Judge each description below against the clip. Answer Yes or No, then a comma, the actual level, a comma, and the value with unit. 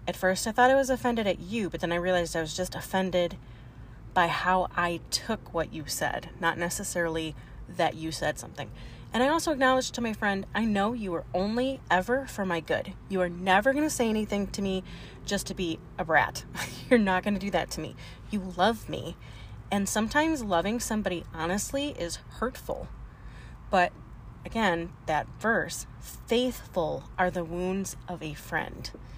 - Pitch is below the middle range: No, medium, 185 Hz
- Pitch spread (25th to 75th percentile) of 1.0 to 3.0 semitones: No, average, 4.6 semitones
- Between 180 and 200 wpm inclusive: Yes, average, 185 wpm